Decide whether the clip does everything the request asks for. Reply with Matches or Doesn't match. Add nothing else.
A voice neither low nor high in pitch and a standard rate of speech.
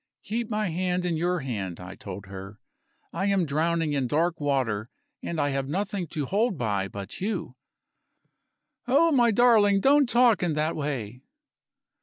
Matches